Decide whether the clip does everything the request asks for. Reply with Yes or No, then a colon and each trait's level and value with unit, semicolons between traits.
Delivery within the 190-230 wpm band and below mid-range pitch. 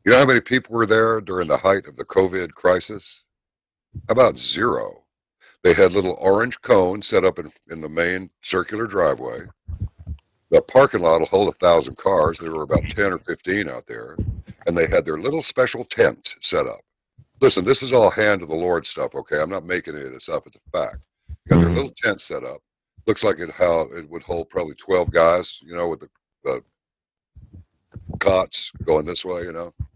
Yes: average, 200 wpm; low, 115 Hz